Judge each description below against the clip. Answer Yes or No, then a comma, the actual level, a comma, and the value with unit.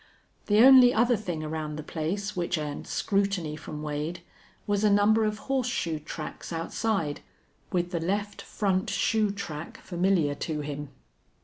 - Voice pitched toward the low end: No, medium, 180 Hz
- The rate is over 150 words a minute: No, average, 145 wpm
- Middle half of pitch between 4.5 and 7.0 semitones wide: Yes, average, 5.1 semitones